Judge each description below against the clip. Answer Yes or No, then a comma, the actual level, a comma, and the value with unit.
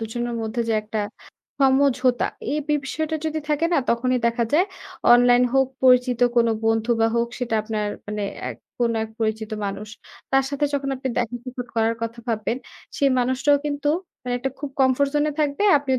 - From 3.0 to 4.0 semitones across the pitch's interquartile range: Yes, average, 3.3 semitones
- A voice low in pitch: No, very high, 250 Hz